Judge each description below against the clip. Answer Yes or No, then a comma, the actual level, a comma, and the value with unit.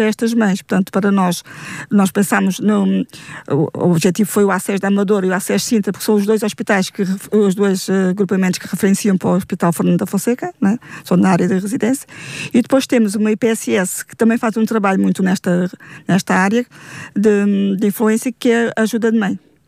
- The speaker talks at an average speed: No, fast, 200 wpm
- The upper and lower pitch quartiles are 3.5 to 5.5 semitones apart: No, average, 2.7 semitones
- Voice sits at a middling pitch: No, high, 200 Hz